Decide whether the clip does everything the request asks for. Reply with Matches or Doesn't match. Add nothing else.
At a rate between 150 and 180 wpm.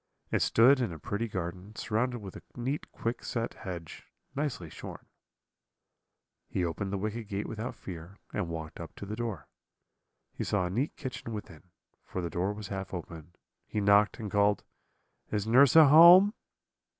Matches